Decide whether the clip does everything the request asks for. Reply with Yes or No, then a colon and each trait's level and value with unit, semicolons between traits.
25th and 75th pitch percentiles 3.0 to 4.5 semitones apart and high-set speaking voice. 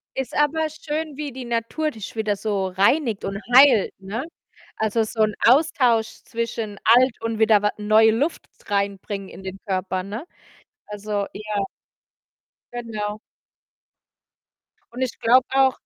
Yes: average, 4.0 semitones; high, 220 Hz